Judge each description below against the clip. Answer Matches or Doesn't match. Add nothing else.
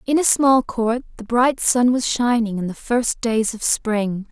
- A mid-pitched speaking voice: Doesn't match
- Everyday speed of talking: Doesn't match